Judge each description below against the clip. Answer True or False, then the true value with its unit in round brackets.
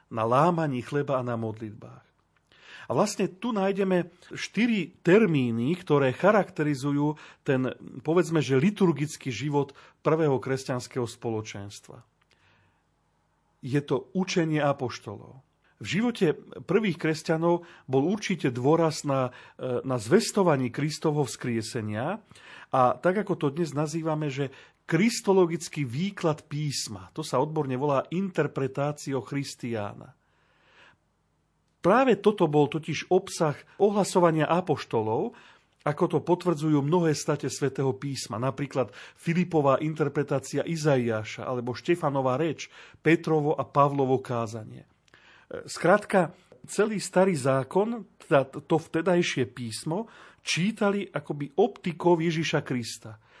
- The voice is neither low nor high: True (150 Hz)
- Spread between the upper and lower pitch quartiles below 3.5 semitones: False (4.7 semitones)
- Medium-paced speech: False (105 wpm)